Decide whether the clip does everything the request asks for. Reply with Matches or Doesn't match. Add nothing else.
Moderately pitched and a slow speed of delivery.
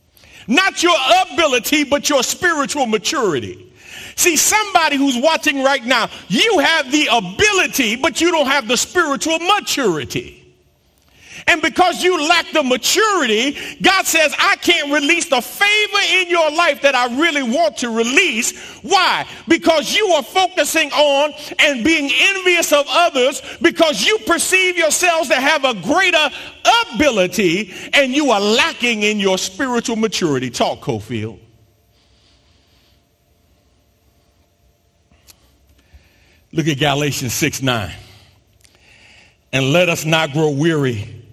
Doesn't match